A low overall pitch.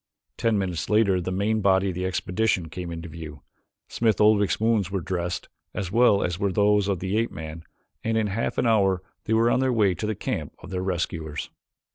Yes: very low, 95 Hz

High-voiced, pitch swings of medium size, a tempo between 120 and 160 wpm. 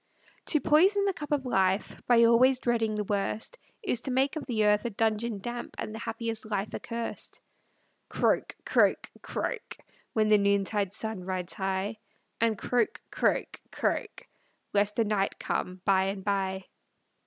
Yes: high, 215 Hz; average, 3.3 semitones; average, 155 wpm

